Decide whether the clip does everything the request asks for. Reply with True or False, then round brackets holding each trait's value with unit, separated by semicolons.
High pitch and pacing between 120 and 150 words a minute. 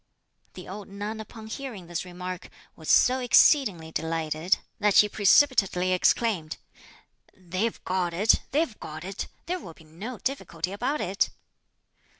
True (195 Hz; 140 wpm)